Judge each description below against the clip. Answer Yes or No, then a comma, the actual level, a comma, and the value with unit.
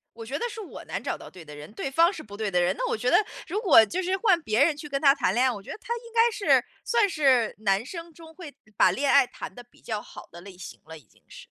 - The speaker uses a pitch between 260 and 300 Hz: Yes, very high, 275 Hz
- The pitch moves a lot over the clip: Yes, wide, 8.9 semitones